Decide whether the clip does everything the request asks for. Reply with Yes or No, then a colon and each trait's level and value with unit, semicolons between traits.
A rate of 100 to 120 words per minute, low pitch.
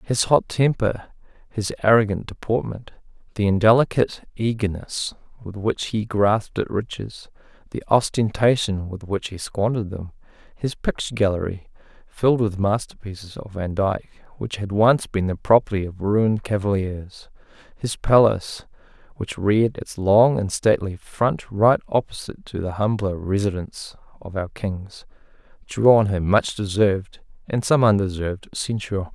No: slow, 135 wpm; low, 105 Hz